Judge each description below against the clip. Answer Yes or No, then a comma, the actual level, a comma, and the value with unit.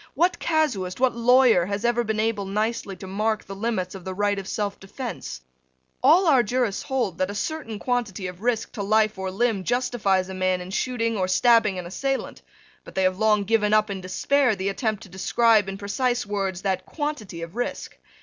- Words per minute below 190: No, average, 195 wpm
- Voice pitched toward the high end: Yes, high, 210 Hz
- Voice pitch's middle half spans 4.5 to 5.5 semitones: No, average, 4.0 semitones